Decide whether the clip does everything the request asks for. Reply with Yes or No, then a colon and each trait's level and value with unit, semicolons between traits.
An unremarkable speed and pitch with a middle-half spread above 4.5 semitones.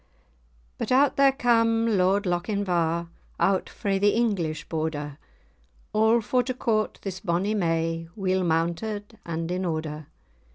No: slow, 130 wpm; average, 5.0 semitones